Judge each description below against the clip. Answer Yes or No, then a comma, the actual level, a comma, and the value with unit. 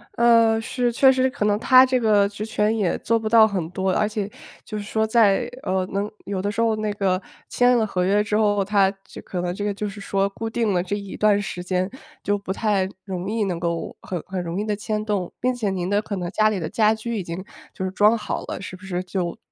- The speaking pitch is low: No, high, 205 Hz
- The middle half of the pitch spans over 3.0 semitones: No, narrow, 2.5 semitones